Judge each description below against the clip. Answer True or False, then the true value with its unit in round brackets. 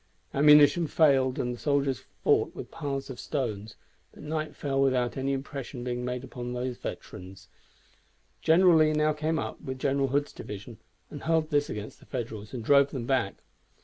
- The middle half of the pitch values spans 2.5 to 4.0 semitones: True (3.2 semitones)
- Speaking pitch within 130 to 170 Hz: True (135 Hz)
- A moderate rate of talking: True (175 wpm)